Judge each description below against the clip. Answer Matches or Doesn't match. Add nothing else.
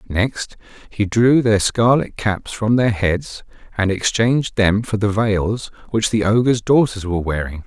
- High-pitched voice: Doesn't match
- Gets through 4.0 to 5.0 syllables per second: Matches